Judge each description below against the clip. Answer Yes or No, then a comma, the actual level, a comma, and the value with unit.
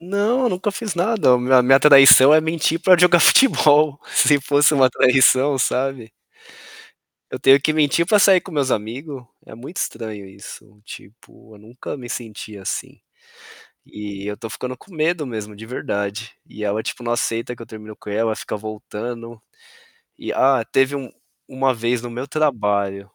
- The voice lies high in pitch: No, low, 130 Hz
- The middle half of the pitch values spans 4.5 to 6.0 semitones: Yes, average, 5.2 semitones